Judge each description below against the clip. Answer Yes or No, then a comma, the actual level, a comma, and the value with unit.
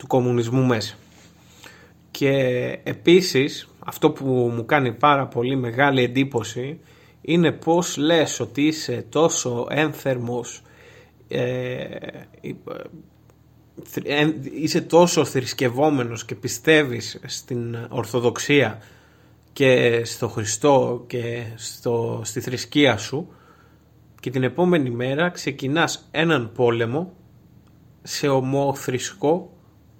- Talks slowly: Yes, slow, 95 wpm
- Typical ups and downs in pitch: Yes, average, 3.9 semitones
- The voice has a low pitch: Yes, low, 130 Hz